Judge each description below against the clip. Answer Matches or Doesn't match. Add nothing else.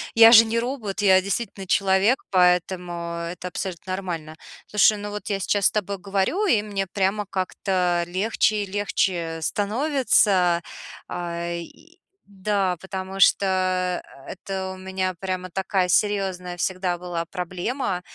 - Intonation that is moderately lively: Doesn't match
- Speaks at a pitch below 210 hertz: Matches